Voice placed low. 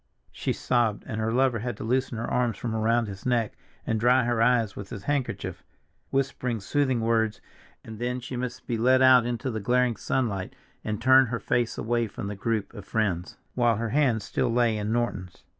Yes: low, 115 Hz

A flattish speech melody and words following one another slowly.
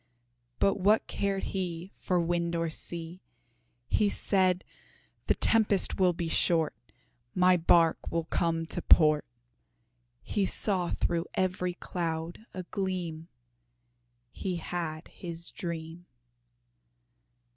Yes: narrow, 2.0 semitones; slow, 110 wpm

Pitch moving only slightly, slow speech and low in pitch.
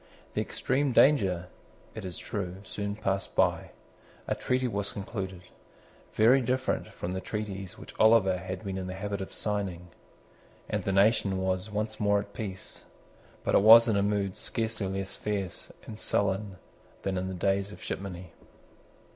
No: narrow, 2.3 semitones; average, 160 wpm; low, 100 Hz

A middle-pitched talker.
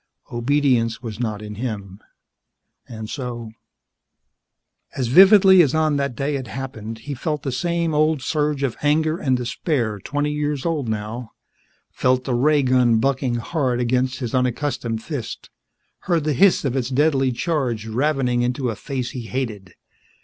No: low, 130 Hz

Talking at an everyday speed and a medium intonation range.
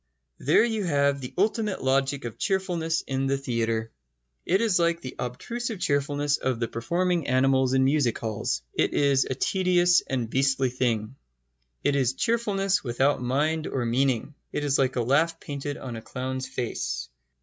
Yes: average, 165 wpm; average, 4.9 semitones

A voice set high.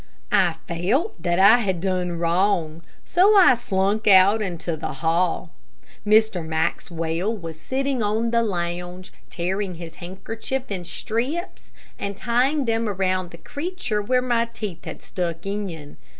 Yes: high, 195 Hz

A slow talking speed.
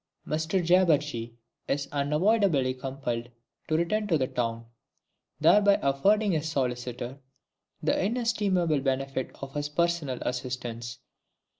Yes: slow, 110 wpm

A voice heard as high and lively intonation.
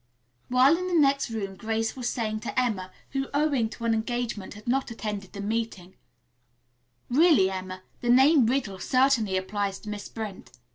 No: high, 225 Hz; average, 4.3 semitones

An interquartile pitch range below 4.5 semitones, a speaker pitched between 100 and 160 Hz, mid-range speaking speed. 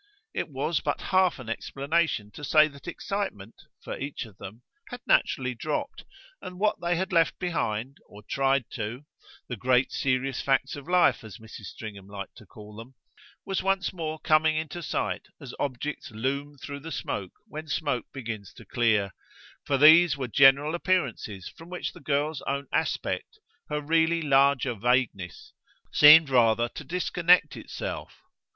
No: wide, 5.4 semitones; medium, 140 Hz; average, 160 wpm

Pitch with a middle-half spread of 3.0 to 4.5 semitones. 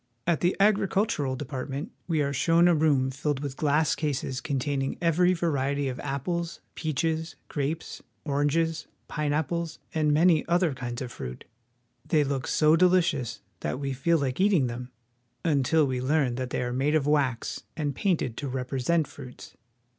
Yes: average, 3.7 semitones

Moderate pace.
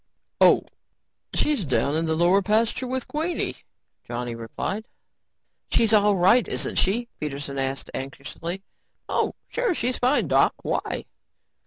No: slow, 130 wpm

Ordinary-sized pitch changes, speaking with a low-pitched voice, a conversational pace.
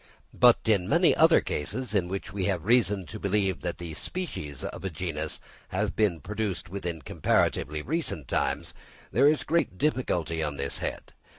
No: wide, 5.9 semitones; very low, 95 Hz; average, 170 wpm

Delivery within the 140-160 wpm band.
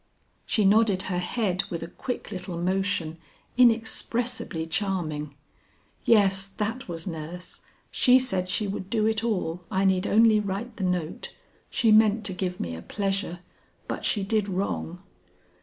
Yes: average, 150 wpm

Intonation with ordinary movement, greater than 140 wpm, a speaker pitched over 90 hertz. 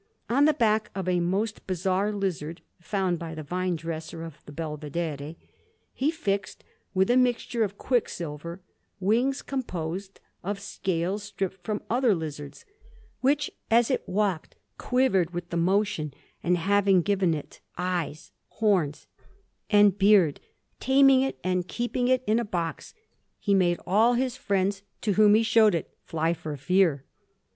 Yes: average, 4.4 semitones; average, 150 wpm; high, 190 Hz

